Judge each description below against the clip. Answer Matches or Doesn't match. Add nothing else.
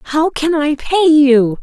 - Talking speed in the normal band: Matches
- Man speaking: Doesn't match